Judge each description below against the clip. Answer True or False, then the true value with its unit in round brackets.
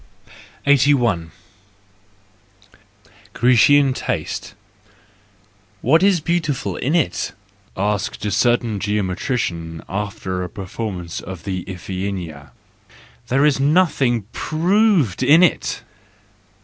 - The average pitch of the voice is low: True (110 Hz)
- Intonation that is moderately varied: False (7.5 semitones)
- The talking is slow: True (90 wpm)